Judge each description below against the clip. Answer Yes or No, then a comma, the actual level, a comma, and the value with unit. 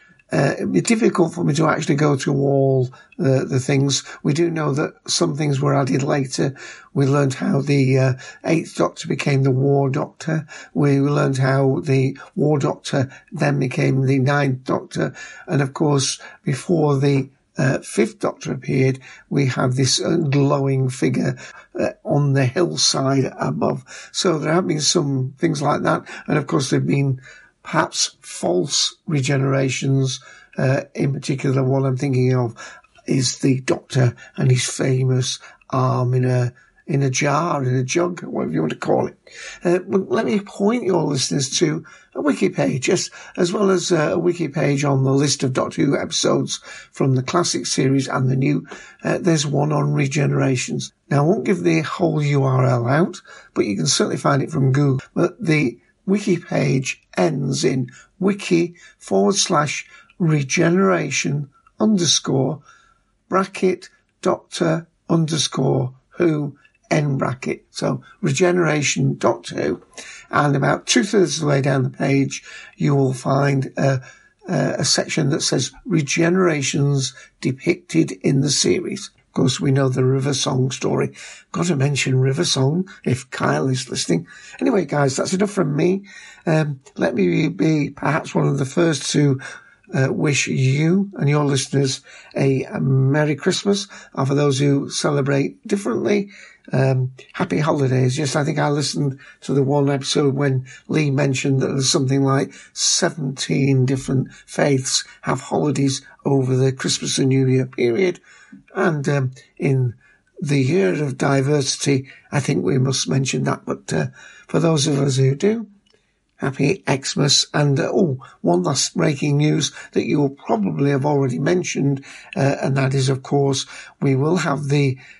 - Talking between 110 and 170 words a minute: Yes, average, 160 wpm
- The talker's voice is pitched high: No, medium, 140 Hz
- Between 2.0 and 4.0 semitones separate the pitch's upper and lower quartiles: Yes, average, 3.5 semitones